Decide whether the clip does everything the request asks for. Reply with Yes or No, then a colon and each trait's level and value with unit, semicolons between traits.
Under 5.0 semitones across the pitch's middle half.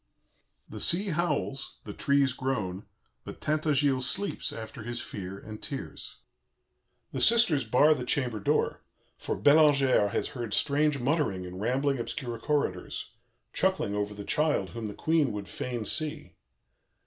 No: wide, 5.6 semitones